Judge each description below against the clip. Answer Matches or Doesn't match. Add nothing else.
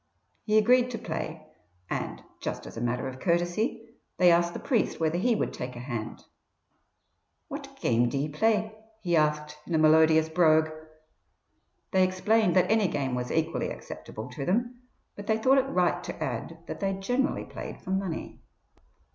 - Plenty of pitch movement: Matches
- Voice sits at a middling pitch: Matches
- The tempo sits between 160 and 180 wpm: Matches